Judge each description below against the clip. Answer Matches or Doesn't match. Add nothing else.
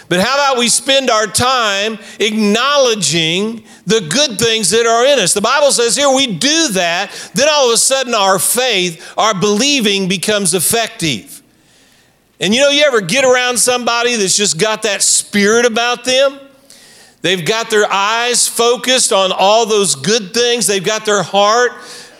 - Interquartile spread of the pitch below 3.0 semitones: Doesn't match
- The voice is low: Doesn't match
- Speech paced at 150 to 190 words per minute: Matches